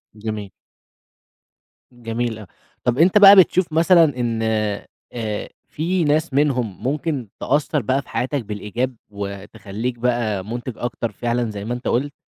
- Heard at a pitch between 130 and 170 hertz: No, low, 120 Hz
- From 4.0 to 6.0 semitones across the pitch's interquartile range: Yes, average, 4.9 semitones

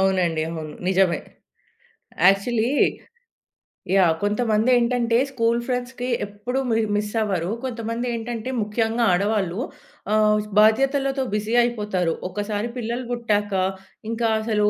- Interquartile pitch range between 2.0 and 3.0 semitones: Yes, average, 2.7 semitones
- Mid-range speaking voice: No, high, 220 Hz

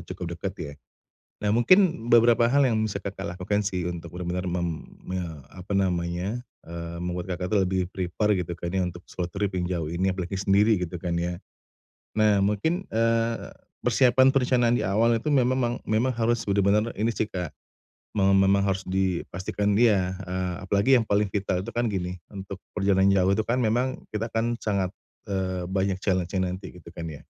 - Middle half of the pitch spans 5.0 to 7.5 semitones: No, average, 3.6 semitones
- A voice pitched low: Yes, very low, 95 Hz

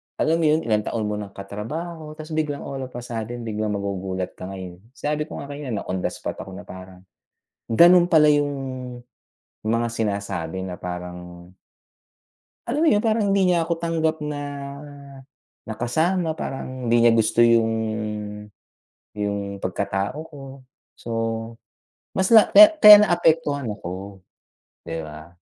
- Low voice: Yes, low, 115 Hz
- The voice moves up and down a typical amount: No, wide, 8.1 semitones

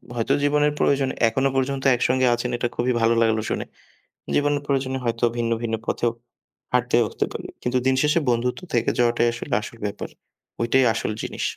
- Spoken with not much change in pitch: Yes, narrow, 2.3 semitones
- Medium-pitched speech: No, low, 125 Hz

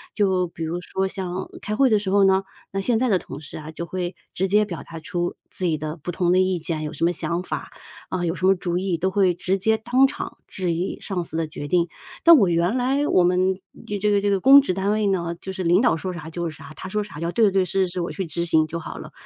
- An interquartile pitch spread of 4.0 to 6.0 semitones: No, narrow, 2.6 semitones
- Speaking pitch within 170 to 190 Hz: Yes, medium, 185 Hz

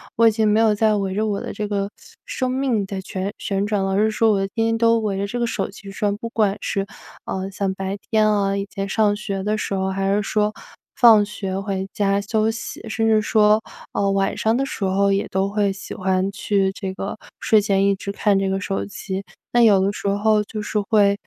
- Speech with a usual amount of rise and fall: No, narrow, 1.8 semitones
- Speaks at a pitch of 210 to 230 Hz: No, high, 200 Hz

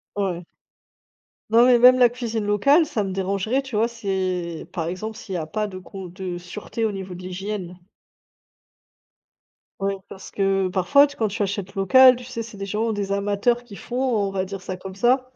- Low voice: No, high, 200 Hz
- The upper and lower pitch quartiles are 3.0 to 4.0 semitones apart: Yes, average, 3.6 semitones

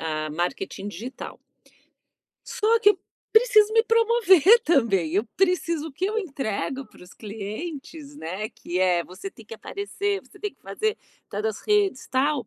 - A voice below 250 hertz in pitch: No, very high, 290 Hz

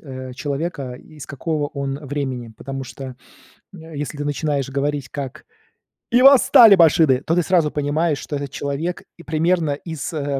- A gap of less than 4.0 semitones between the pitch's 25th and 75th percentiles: Yes, average, 2.8 semitones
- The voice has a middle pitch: Yes, medium, 145 Hz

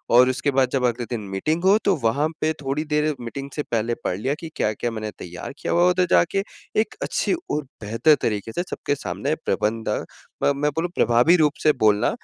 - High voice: No, low, 135 Hz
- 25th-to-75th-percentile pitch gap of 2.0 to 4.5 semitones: No, average, 5.3 semitones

